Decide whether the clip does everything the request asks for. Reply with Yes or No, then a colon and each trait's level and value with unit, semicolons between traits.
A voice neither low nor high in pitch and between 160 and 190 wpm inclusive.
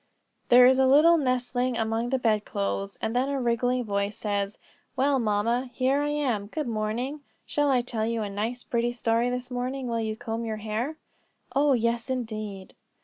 No: high, 240 Hz; average, 185 wpm